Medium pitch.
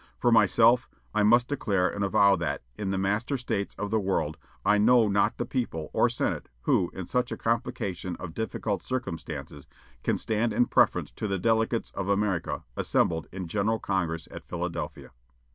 No: low, 100 Hz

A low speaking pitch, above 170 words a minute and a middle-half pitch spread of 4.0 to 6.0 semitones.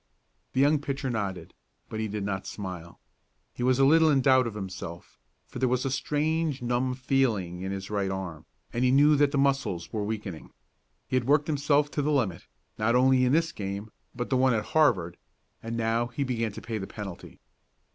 Yes: low, 120 Hz; fast, 205 wpm; average, 5.3 semitones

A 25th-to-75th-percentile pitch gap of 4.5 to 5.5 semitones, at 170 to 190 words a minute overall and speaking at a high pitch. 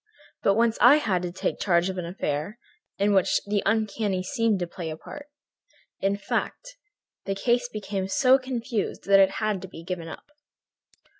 No: average, 3.8 semitones; average, 175 wpm; high, 200 Hz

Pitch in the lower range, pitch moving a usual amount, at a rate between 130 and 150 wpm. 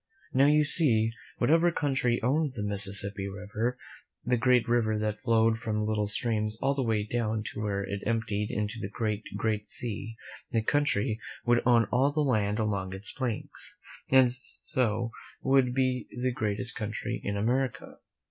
No: low, 115 Hz; average, 3.1 semitones; average, 160 wpm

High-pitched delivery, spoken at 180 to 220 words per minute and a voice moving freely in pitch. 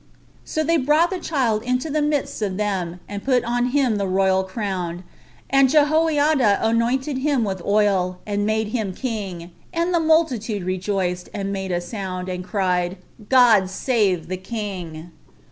No: high, 210 Hz; average, 160 wpm; wide, 5.9 semitones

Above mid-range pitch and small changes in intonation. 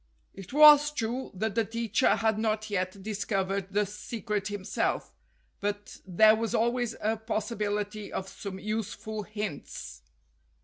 Yes: high, 215 Hz; narrow, 1.9 semitones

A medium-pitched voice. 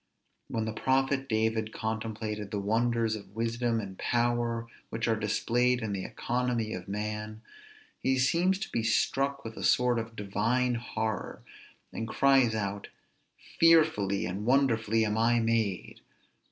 No: low, 115 Hz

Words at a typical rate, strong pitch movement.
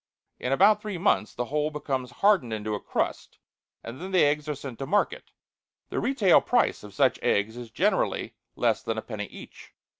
Yes: average, 190 wpm; wide, 8.0 semitones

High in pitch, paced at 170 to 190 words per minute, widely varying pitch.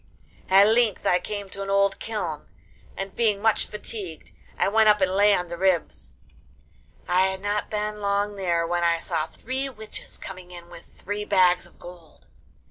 No: high, 195 Hz; average, 180 wpm; average, 2.8 semitones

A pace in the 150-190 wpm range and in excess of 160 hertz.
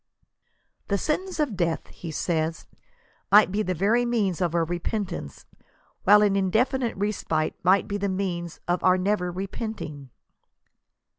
No: average, 140 wpm; high, 190 Hz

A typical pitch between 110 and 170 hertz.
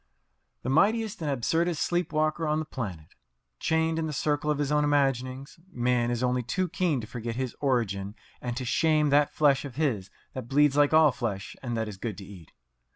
Yes: low, 135 Hz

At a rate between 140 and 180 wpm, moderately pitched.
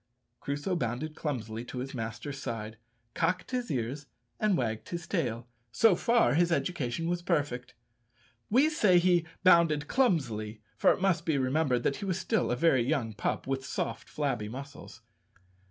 Yes: average, 160 wpm; medium, 145 Hz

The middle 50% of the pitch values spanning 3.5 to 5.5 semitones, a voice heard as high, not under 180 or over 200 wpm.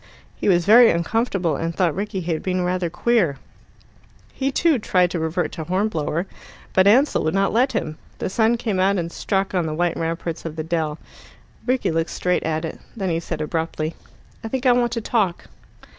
No: average, 4.9 semitones; medium, 180 Hz; average, 195 wpm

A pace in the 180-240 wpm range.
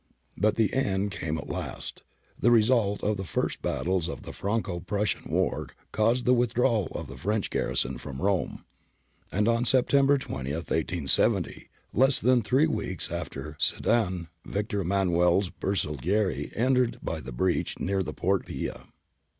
No: average, 155 wpm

